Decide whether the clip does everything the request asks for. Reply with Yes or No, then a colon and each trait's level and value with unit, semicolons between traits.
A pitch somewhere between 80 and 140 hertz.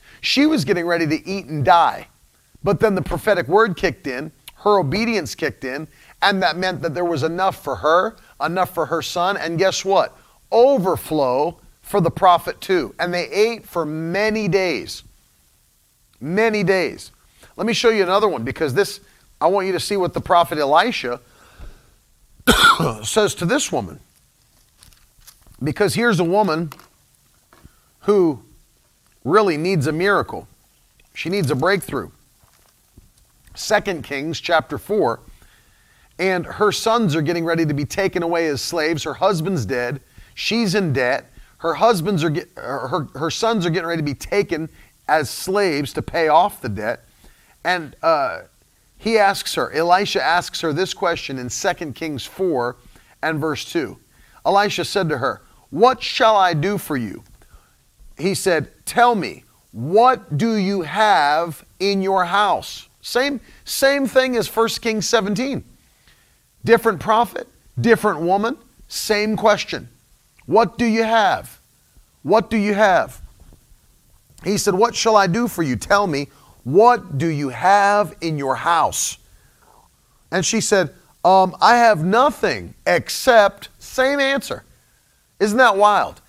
No: high, 190 Hz